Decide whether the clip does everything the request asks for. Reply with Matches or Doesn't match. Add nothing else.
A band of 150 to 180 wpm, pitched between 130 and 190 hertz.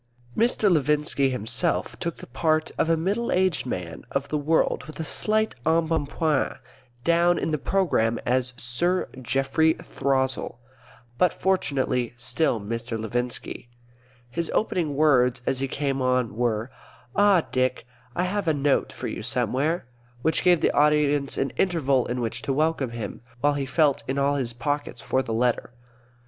Matches